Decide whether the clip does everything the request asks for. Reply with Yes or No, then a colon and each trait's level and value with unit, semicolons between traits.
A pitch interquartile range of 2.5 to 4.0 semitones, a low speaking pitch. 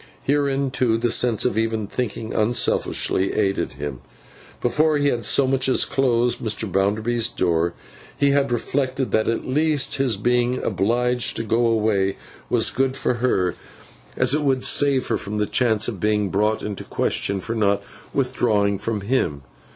Yes: average, 3.7 semitones; low, 115 Hz